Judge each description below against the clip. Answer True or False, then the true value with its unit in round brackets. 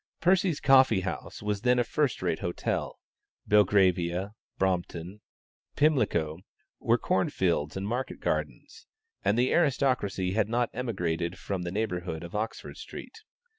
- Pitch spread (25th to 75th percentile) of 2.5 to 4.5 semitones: False (5.6 semitones)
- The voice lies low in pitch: True (100 Hz)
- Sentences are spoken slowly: True (130 wpm)